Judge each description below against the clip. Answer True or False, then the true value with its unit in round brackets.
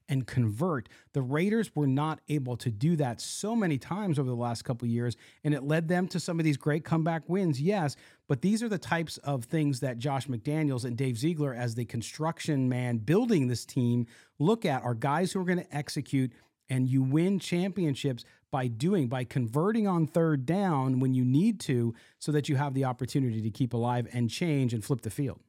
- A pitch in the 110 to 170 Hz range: True (140 Hz)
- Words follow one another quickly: True (210 wpm)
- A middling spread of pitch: True (4.5 semitones)